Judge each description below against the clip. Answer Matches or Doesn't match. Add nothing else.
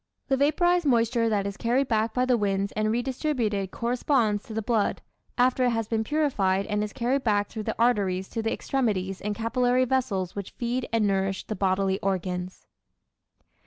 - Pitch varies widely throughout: Doesn't match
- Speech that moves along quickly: Doesn't match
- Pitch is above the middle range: Matches